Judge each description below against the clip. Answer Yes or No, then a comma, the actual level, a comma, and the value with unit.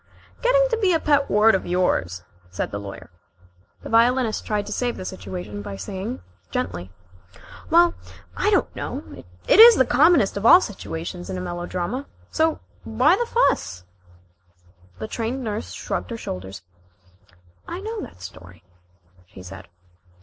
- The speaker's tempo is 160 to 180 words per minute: No, average, 150 wpm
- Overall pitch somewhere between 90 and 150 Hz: No, high, 205 Hz